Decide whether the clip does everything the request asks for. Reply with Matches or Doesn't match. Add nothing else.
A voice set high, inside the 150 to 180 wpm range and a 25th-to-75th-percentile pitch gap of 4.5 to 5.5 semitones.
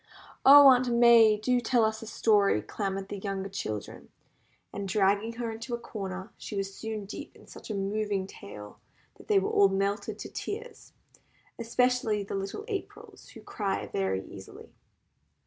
Doesn't match